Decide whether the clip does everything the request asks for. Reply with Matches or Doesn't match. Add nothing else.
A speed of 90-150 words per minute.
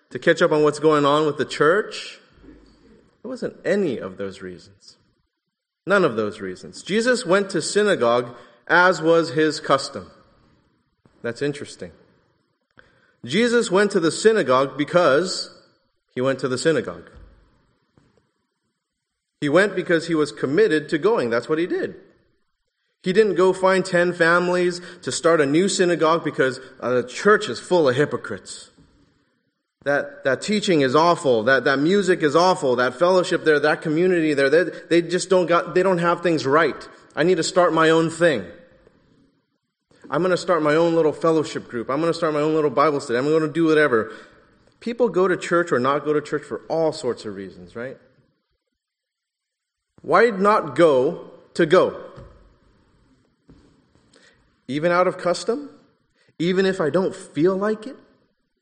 Doesn't match